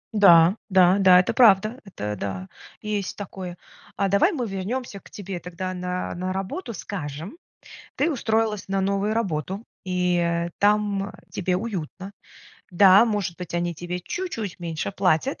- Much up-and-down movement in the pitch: No, average, 2.9 semitones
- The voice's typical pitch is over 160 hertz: Yes, high, 190 Hz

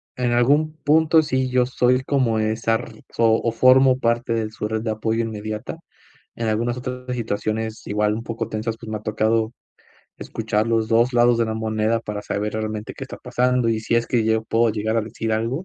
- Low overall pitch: Yes, low, 115 Hz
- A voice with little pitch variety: Yes, narrow, 2.0 semitones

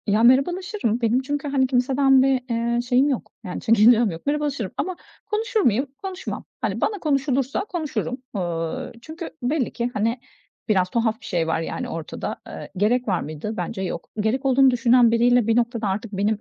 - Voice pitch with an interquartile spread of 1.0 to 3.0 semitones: No, average, 4.1 semitones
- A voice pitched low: No, high, 245 Hz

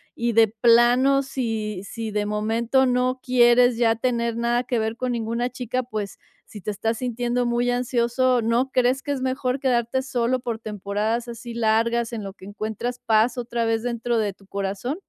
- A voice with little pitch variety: Yes, narrow, 2.0 semitones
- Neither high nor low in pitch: No, high, 235 Hz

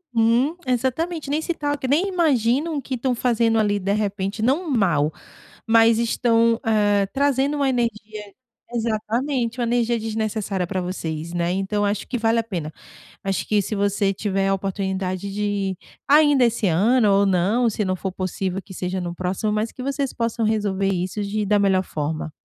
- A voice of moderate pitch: No, high, 215 Hz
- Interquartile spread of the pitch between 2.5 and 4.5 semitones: Yes, average, 3.9 semitones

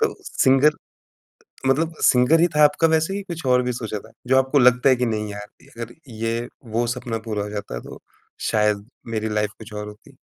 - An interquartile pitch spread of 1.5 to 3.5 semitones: No, average, 4.0 semitones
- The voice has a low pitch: Yes, low, 120 Hz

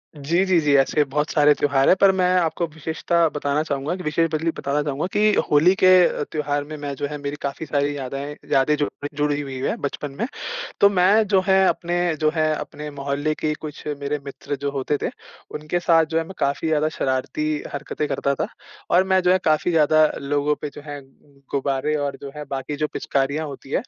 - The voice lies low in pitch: No, medium, 150 Hz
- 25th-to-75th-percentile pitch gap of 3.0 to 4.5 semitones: No, narrow, 2.4 semitones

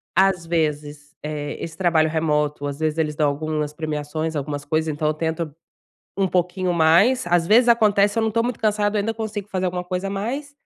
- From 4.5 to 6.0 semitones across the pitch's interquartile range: Yes, average, 4.8 semitones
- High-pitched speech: No, medium, 165 Hz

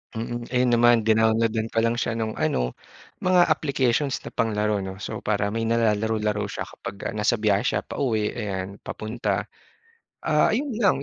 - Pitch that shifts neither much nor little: No, narrow, 2.2 semitones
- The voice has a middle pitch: No, low, 110 Hz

